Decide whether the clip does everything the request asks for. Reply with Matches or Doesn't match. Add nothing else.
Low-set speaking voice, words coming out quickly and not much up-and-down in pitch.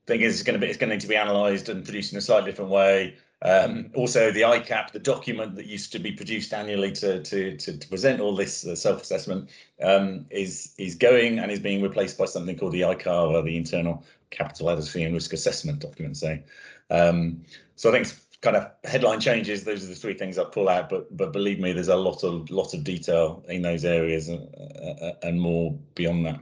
Doesn't match